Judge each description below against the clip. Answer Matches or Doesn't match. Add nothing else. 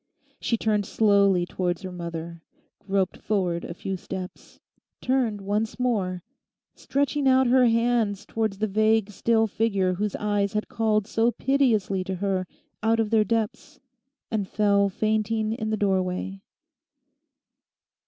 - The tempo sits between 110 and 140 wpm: Matches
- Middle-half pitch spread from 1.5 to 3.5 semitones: Matches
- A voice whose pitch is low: Doesn't match